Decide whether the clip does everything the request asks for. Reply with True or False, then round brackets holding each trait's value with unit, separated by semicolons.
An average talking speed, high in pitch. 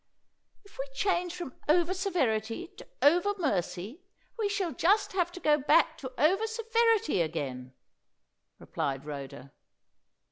False (130 wpm; 330 Hz)